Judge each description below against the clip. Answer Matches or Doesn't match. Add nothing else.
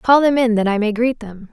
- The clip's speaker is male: Doesn't match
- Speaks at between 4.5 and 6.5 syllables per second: Matches